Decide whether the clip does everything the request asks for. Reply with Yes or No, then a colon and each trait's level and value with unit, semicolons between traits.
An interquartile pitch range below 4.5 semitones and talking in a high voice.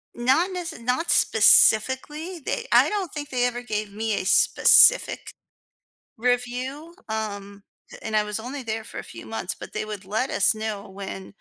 No: average, 4.8 semitones; high, 240 Hz